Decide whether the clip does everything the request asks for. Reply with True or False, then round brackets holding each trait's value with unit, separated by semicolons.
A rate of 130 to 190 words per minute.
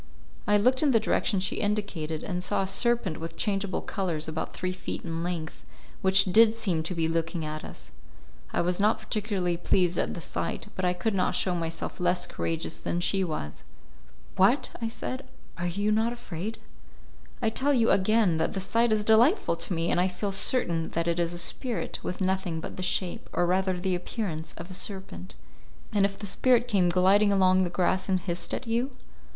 False (200 wpm)